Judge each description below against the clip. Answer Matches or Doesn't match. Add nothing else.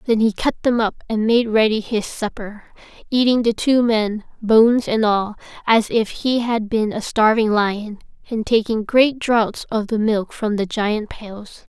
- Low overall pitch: Doesn't match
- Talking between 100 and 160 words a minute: Doesn't match